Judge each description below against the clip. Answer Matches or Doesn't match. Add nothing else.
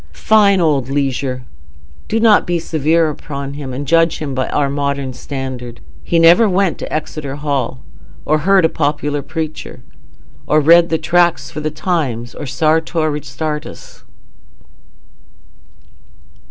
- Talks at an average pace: Doesn't match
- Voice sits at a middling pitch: Matches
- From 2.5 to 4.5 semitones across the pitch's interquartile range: Matches